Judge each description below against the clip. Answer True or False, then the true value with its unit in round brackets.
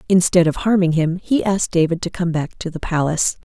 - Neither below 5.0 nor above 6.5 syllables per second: True (6.0 syllables/s)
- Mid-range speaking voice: True (175 Hz)